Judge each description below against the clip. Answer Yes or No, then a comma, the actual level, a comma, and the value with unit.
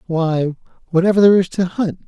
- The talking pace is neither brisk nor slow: Yes, average, 175 wpm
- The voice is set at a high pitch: No, medium, 175 Hz